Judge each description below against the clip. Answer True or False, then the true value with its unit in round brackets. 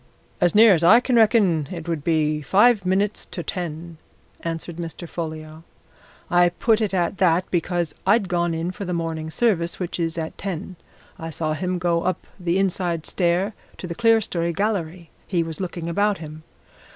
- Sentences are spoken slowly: False (175 wpm)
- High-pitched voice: False (175 Hz)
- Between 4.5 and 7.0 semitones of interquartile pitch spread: False (2.8 semitones)